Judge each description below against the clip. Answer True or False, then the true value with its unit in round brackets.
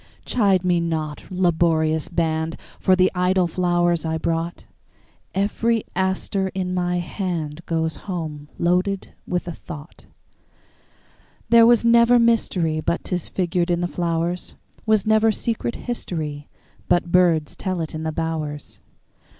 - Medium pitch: True (175 Hz)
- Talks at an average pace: False (110 wpm)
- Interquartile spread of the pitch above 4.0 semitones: False (2.6 semitones)